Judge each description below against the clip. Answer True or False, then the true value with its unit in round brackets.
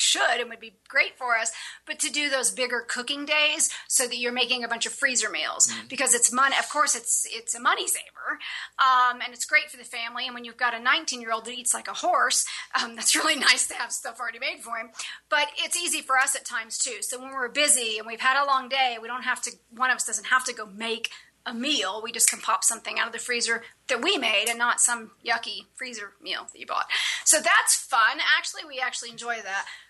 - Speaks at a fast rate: True (250 wpm)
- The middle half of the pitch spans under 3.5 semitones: True (2.8 semitones)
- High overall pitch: True (245 Hz)